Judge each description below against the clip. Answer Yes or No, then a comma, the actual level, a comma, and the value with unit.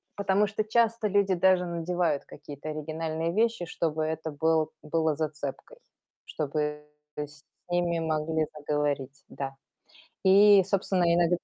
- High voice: No, medium, 160 Hz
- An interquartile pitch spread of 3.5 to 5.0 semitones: Yes, average, 3.8 semitones